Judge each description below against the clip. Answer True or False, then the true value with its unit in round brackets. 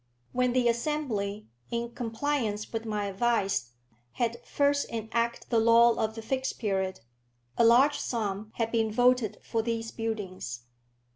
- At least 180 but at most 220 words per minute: False (140 wpm)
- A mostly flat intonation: True (2.1 semitones)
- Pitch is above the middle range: True (230 Hz)